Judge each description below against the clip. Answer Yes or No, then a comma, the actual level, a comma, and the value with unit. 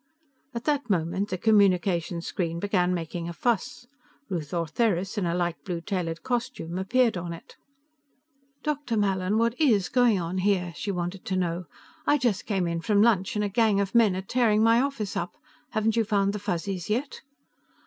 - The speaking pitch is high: Yes, high, 195 Hz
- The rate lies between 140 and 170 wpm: No, average, 185 wpm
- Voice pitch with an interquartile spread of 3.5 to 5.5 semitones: Yes, average, 4.2 semitones